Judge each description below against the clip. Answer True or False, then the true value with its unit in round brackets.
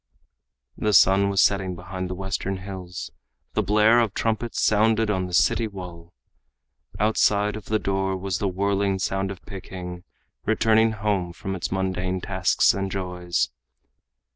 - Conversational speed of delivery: True (145 wpm)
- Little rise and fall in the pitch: True (2.2 semitones)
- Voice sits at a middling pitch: False (95 Hz)